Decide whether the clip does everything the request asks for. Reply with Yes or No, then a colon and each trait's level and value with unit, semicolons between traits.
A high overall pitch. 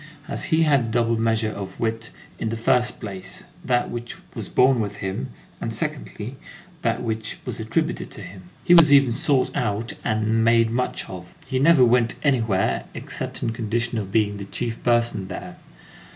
No: low, 115 Hz